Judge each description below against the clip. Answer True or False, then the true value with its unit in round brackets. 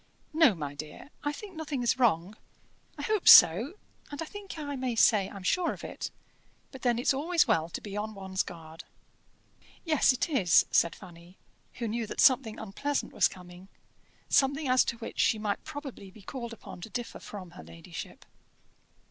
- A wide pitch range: True (7.2 semitones)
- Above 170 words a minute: True (180 wpm)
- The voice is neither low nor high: False (230 Hz)